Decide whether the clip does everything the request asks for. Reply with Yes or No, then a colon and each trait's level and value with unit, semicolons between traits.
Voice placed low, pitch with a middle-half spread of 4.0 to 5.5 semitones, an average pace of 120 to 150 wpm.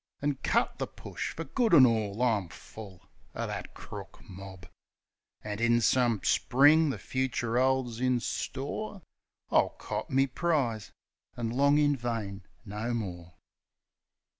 Yes: low, 120 Hz; average, 4.4 semitones; average, 140 wpm